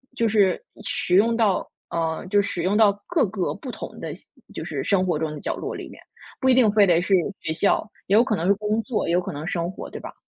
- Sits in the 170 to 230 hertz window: Yes, high, 200 Hz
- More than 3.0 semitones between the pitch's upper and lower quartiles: Yes, average, 3.8 semitones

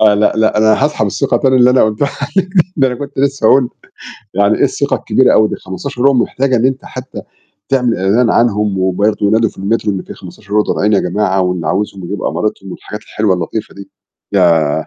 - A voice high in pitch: No, low, 105 Hz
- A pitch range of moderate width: Yes, average, 4.3 semitones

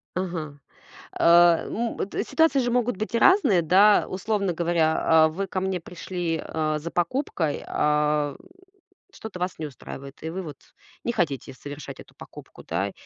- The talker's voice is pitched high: No, medium, 175 Hz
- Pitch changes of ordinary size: Yes, average, 4.2 semitones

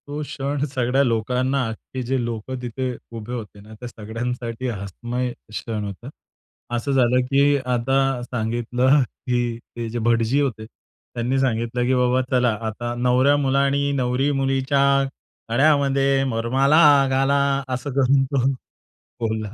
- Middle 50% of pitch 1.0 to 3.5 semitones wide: Yes, narrow, 2.6 semitones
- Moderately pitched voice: No, low, 125 Hz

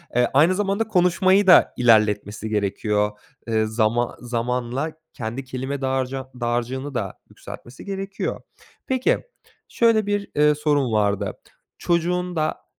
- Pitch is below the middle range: Yes, low, 130 Hz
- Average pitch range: No, wide, 7.9 semitones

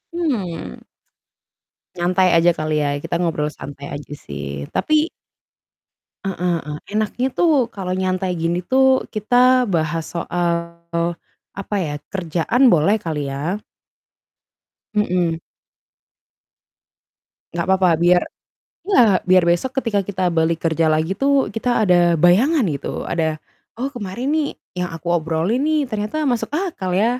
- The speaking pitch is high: No, medium, 180 Hz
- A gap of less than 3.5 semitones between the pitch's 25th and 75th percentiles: No, average, 4.8 semitones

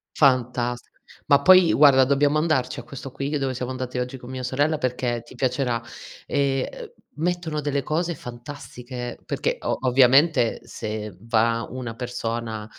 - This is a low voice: Yes, low, 130 Hz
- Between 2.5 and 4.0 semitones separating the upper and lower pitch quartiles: Yes, average, 2.9 semitones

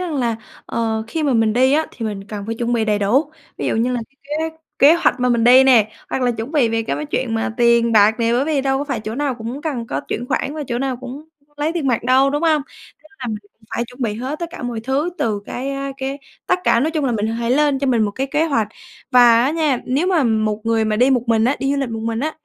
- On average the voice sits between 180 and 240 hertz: No, very high, 250 Hz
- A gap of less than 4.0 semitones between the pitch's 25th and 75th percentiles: Yes, average, 3.6 semitones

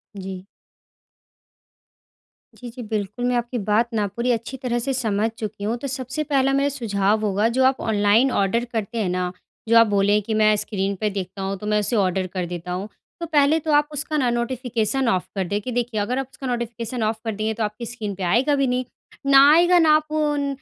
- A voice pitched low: No, high, 230 Hz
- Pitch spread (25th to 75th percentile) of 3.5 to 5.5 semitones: Yes, average, 4.3 semitones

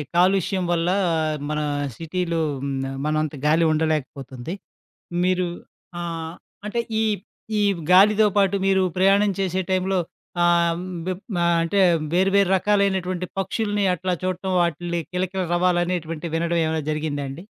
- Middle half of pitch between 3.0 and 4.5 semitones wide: No, narrow, 2.5 semitones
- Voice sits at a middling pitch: Yes, medium, 180 Hz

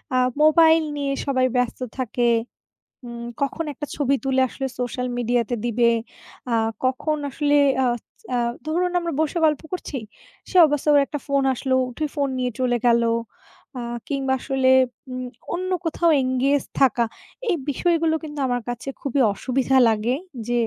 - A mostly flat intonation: No, average, 3.4 semitones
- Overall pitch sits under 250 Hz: No, very high, 270 Hz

